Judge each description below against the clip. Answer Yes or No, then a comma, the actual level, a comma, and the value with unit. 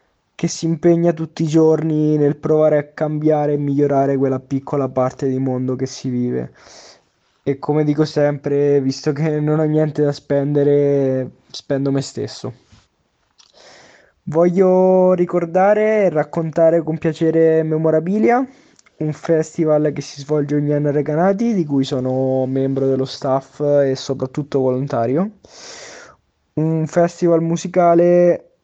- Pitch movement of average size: Yes, average, 3.2 semitones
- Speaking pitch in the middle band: Yes, medium, 150 Hz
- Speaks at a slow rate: No, average, 130 wpm